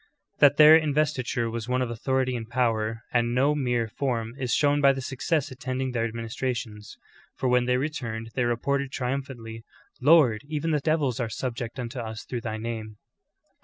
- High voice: No, low, 125 Hz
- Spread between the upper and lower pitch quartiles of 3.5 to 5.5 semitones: No, average, 3.1 semitones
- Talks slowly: No, average, 175 wpm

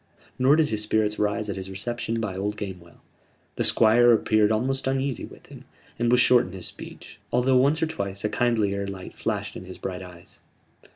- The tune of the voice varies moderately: Yes, average, 3.9 semitones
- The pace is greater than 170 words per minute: Yes, average, 195 wpm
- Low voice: Yes, low, 110 Hz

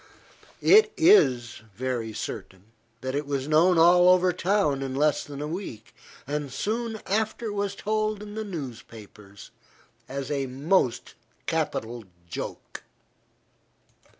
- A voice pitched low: No, medium, 150 Hz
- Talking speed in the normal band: No, slow, 125 wpm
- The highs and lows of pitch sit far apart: Yes, wide, 7.9 semitones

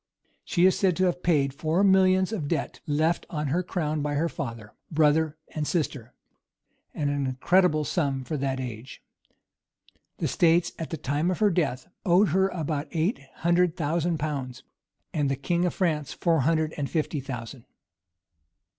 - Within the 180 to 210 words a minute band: No, average, 165 wpm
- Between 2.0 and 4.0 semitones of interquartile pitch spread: Yes, average, 3.6 semitones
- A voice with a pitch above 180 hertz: No, medium, 155 Hz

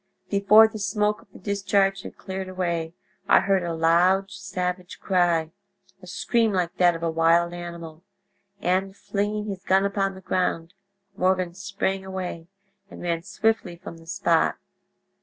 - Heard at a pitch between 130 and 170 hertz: No, medium, 185 Hz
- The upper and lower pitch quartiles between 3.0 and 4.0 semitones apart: No, narrow, 2.5 semitones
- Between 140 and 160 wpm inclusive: Yes, average, 145 wpm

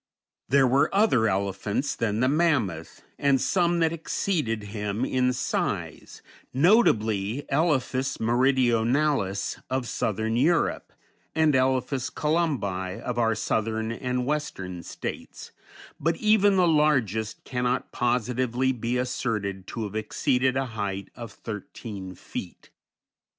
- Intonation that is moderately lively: Yes, average, 4.4 semitones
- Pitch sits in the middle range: No, low, 125 Hz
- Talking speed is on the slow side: Yes, slow, 115 wpm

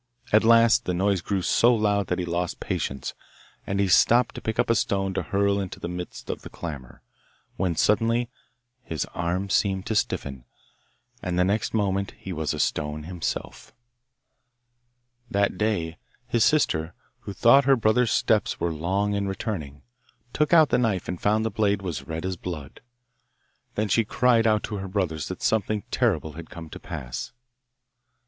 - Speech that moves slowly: No, average, 175 wpm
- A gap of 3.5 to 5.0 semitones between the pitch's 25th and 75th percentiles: Yes, average, 4.1 semitones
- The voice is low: Yes, low, 100 Hz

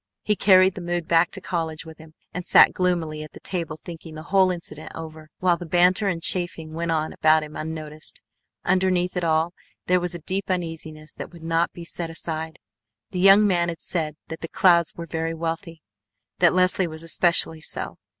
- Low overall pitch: No, medium, 170 Hz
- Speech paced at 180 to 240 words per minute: Yes, average, 200 wpm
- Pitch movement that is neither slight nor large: No, narrow, 2.1 semitones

